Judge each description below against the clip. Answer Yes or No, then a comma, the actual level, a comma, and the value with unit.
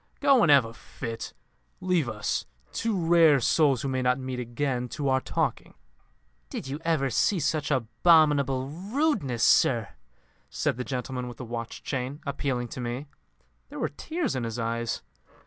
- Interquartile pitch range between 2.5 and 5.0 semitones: Yes, average, 4.3 semitones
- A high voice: No, low, 135 Hz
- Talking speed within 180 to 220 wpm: No, average, 165 wpm